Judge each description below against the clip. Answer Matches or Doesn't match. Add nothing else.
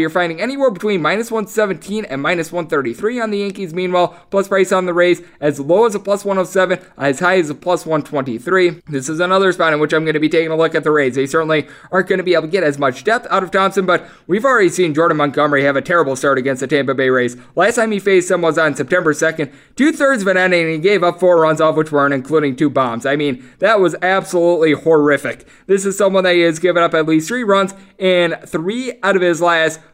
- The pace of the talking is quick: Matches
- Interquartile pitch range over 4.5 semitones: Doesn't match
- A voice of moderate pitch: Matches